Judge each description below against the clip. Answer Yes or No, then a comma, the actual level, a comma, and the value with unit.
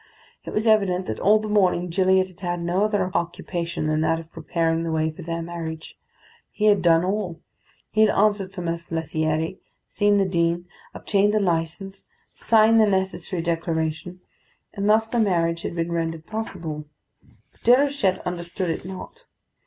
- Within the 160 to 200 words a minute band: Yes, average, 170 wpm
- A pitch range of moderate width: Yes, average, 3.6 semitones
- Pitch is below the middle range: No, medium, 180 Hz